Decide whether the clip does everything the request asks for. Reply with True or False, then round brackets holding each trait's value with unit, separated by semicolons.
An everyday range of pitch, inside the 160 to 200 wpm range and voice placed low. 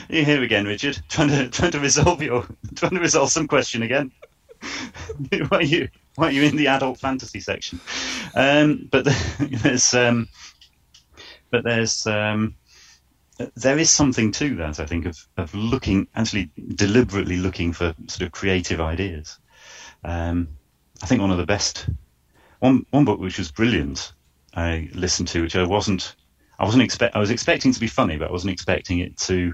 False (7.0 semitones; 185 wpm; 105 Hz)